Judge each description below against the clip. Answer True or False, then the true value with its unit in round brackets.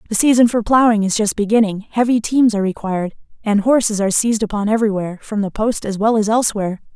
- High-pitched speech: True (215 Hz)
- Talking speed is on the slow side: False (205 wpm)